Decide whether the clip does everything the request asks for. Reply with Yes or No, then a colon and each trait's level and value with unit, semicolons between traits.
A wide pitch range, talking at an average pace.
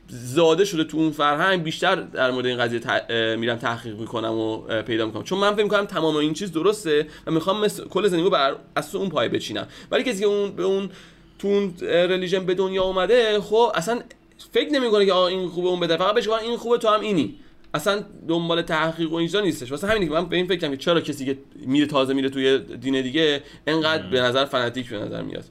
No: wide, 6.4 semitones; fast, 215 wpm